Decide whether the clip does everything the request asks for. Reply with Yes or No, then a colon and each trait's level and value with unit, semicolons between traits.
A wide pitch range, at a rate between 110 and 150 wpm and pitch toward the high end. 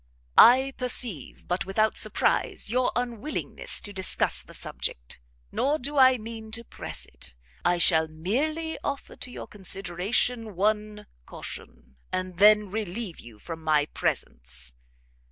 Yes: wide, 6.1 semitones; slow, 135 wpm; high, 210 Hz